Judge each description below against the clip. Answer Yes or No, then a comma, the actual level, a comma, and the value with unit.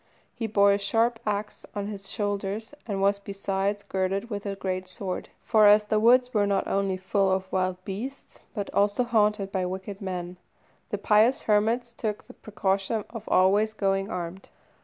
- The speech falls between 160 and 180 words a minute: Yes, average, 175 wpm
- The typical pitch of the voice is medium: No, high, 200 Hz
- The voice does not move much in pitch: Yes, narrow, 1.8 semitones